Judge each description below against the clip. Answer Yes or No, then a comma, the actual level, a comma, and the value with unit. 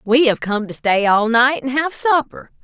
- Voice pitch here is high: Yes, very high, 250 Hz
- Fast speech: Yes, fast, 230 wpm